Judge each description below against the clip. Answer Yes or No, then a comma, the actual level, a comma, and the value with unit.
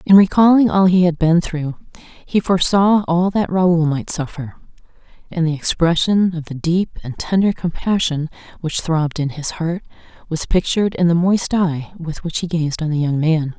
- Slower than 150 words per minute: No, average, 185 wpm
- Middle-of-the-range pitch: Yes, medium, 170 Hz